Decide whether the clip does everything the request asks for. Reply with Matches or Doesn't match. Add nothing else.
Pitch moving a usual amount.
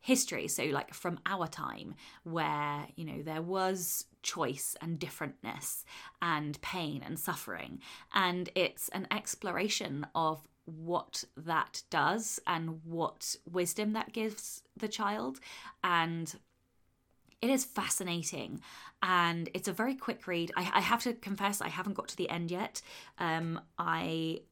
Matches